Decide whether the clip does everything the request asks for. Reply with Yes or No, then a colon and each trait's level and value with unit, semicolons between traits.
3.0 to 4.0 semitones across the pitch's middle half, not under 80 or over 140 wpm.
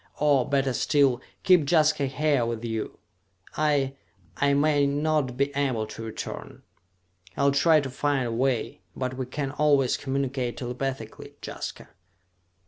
No: narrow, 2.4 semitones; slow, 135 wpm